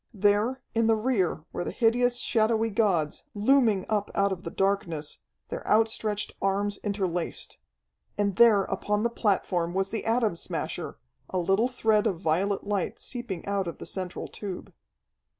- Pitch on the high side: Yes, high, 205 Hz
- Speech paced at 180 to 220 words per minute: No, average, 155 wpm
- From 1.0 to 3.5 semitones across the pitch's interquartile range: Yes, average, 2.9 semitones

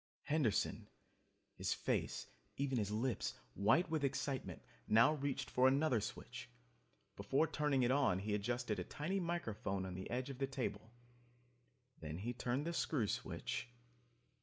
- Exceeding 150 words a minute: No, average, 145 wpm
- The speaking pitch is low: Yes, low, 130 Hz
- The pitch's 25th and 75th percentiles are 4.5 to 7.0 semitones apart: Yes, average, 5.0 semitones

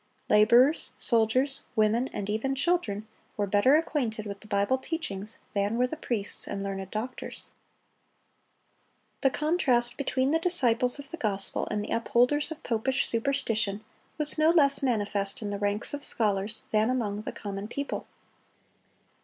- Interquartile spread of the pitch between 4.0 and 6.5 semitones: Yes, average, 5.0 semitones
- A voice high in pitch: Yes, high, 230 Hz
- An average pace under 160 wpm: Yes, average, 150 wpm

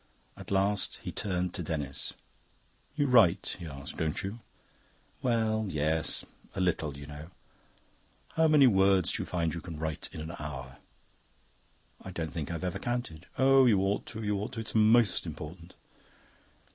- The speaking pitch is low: Yes, very low, 90 Hz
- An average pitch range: No, wide, 5.7 semitones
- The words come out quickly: No, average, 165 wpm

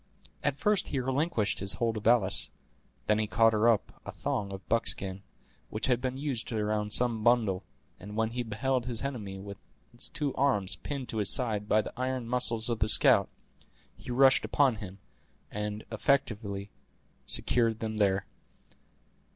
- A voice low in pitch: Yes, low, 110 Hz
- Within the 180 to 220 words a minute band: No, average, 165 wpm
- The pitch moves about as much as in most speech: Yes, average, 3.2 semitones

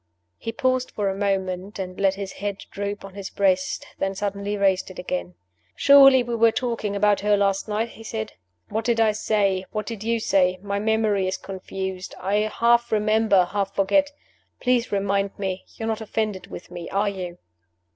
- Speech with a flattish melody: Yes, narrow, 2.3 semitones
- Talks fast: No, average, 185 wpm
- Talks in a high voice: Yes, high, 200 Hz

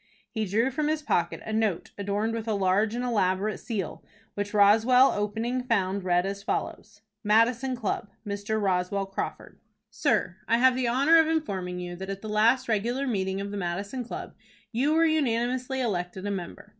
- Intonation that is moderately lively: Yes, average, 4.0 semitones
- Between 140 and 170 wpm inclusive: No, average, 180 wpm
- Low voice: No, high, 215 Hz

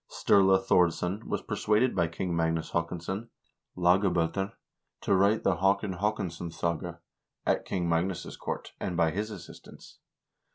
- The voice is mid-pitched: No, very low, 90 Hz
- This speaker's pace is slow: Yes, slow, 125 wpm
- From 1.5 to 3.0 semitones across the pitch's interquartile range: Yes, narrow, 2.6 semitones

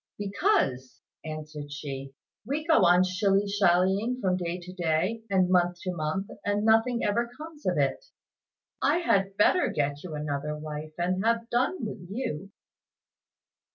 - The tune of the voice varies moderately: No, wide, 6.3 semitones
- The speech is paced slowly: No, average, 150 wpm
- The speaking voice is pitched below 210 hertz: Yes, medium, 185 Hz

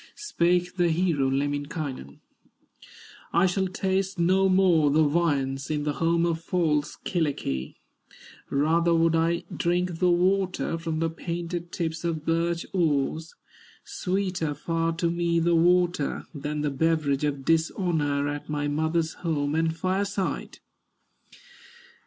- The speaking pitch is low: No, medium, 165 Hz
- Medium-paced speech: No, slow, 130 wpm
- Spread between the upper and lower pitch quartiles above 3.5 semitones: No, average, 2.9 semitones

